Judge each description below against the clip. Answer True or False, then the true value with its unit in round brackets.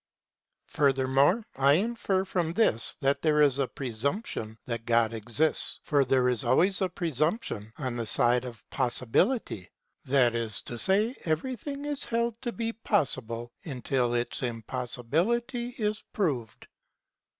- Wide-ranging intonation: True (8.8 semitones)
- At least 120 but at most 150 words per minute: True (140 wpm)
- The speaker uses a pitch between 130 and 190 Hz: True (140 Hz)